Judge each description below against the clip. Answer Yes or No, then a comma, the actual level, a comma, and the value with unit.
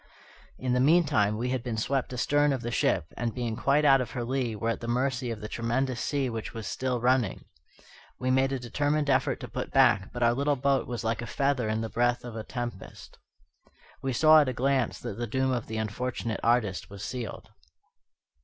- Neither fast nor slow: No, fast, 215 wpm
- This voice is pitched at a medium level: No, low, 125 Hz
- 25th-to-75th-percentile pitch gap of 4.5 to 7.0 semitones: No, narrow, 2.6 semitones